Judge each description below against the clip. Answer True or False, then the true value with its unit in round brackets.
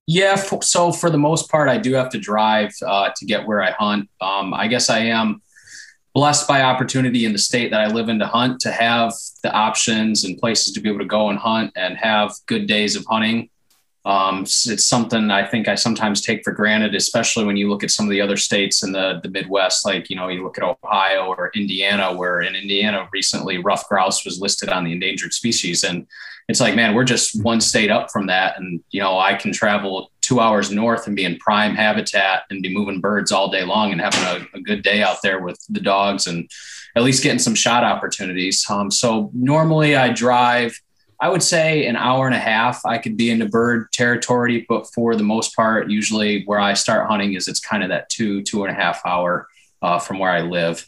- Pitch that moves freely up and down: False (3.4 semitones)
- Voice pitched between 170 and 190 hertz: False (105 Hz)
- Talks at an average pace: False (230 wpm)